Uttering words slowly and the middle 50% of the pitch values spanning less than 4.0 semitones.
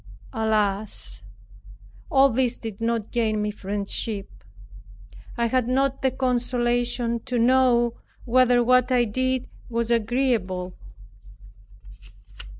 Yes: slow, 100 wpm; narrow, 2.6 semitones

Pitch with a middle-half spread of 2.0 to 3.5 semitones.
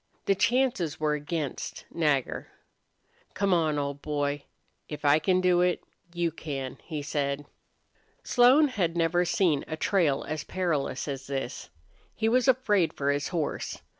No: average, 4.3 semitones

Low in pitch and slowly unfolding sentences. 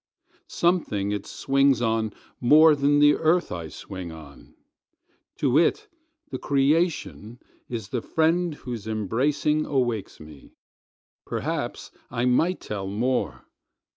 Yes: low, 125 Hz; slow, 105 wpm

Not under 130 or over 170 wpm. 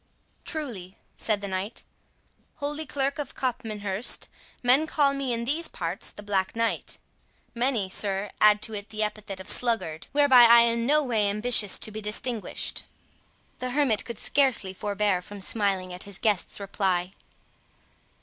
Yes: average, 150 wpm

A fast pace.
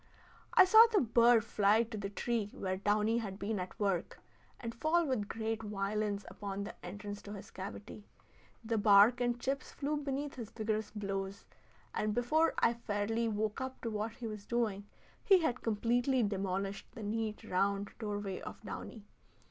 No: average, 170 wpm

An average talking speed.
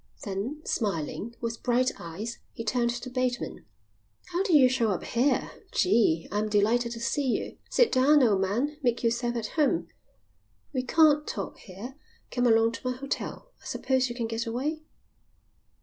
Yes: average, 170 wpm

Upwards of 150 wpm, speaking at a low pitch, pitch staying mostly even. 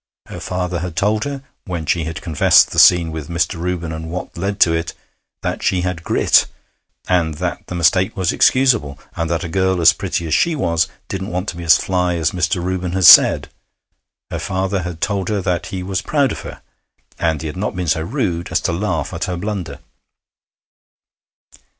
Yes: average, 200 wpm; very low, 90 Hz; narrow, 2.3 semitones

